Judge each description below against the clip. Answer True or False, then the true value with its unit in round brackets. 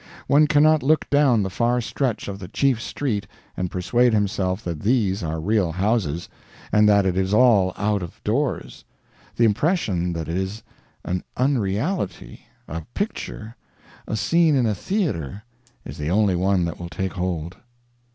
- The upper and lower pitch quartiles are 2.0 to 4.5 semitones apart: False (5.2 semitones)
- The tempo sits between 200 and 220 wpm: False (160 wpm)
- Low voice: True (105 Hz)